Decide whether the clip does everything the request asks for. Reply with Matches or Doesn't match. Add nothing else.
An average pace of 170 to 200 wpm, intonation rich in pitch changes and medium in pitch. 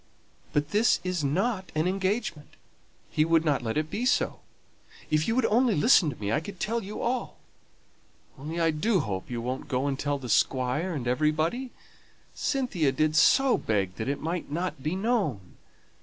Matches